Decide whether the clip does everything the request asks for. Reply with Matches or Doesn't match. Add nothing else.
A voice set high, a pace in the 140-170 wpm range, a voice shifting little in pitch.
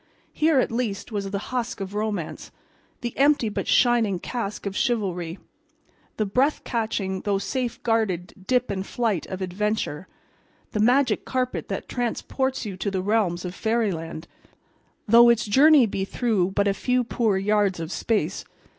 Doesn't match